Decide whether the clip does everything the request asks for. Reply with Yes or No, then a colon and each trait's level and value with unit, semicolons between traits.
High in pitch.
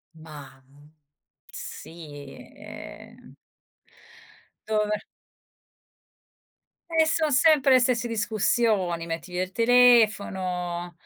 Yes: high, 210 Hz